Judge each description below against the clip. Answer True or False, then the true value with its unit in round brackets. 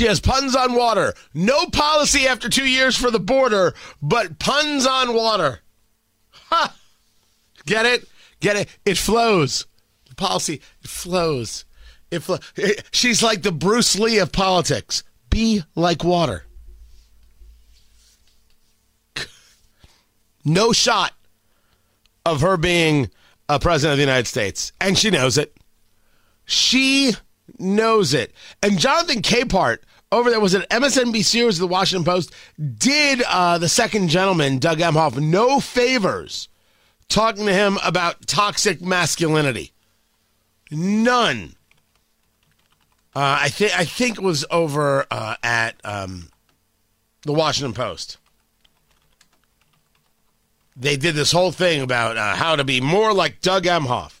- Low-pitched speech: False (170 Hz)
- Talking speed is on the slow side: True (130 wpm)